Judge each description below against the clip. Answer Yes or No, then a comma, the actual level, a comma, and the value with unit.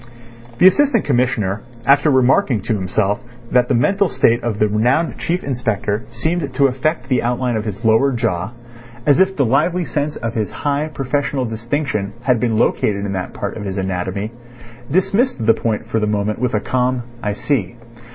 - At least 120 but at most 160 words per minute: No, average, 180 wpm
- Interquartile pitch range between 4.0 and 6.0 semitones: Yes, average, 4.9 semitones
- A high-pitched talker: No, low, 120 Hz